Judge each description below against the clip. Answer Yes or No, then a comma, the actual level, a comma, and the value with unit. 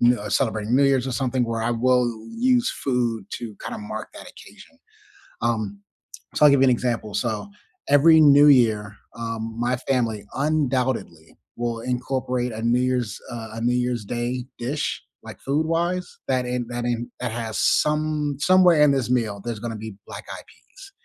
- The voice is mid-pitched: No, low, 125 Hz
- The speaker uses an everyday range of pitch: Yes, average, 3.3 semitones